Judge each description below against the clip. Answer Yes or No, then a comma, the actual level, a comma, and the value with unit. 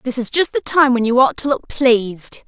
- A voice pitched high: Yes, very high, 255 Hz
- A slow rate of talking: No, fast, 265 wpm